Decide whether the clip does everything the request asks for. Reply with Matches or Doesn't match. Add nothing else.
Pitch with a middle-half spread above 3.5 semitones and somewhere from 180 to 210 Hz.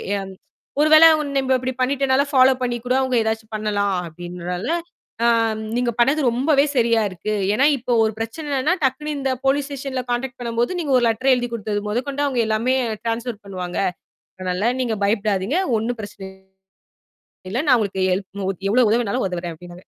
Doesn't match